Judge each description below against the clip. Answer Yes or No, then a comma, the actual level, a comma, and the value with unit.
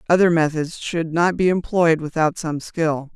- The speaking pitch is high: No, medium, 165 Hz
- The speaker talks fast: No, average, 170 wpm